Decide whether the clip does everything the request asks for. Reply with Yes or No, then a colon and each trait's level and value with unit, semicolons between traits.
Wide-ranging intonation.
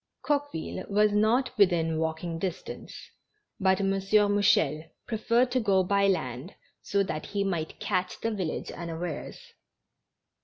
No: average, 3.9 semitones